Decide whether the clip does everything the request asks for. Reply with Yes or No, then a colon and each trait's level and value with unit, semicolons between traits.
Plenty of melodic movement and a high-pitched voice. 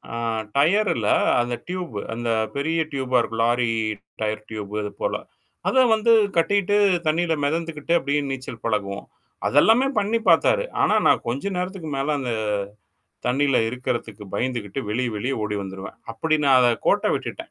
No: wide, 6.3 semitones; low, 135 Hz